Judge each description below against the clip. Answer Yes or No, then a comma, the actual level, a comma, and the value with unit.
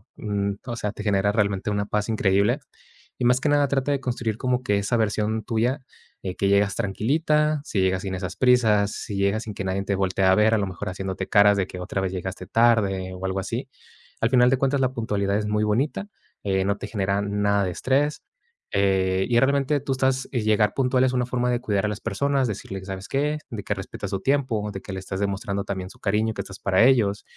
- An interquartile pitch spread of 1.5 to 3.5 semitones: No, average, 4.2 semitones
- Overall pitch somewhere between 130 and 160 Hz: No, low, 105 Hz